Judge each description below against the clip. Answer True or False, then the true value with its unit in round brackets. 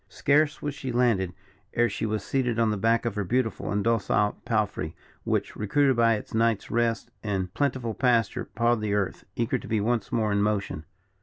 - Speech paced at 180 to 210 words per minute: True (190 wpm)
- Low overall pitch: True (115 Hz)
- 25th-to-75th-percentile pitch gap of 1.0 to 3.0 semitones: True (2.5 semitones)